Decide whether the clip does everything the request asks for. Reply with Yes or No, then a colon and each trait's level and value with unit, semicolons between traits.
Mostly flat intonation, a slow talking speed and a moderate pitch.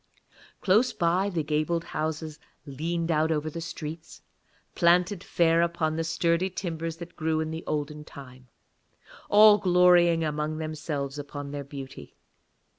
Yes: narrow, 2.1 semitones; slow, 130 wpm; medium, 160 Hz